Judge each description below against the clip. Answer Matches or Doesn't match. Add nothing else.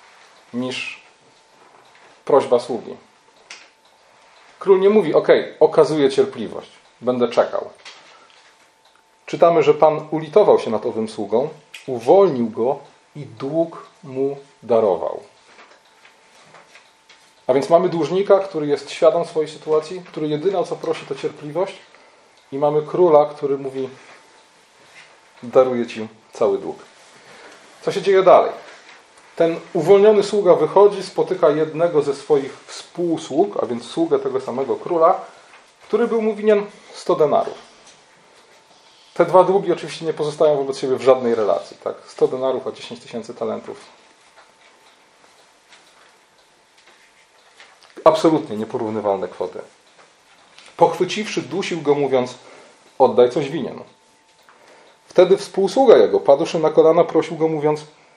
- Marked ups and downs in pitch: Matches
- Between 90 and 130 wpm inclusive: Matches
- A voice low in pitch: Doesn't match